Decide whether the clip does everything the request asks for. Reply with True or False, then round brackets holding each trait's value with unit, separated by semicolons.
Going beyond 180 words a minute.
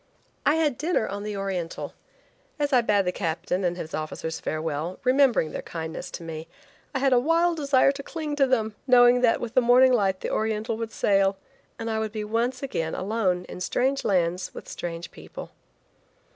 True (190 wpm)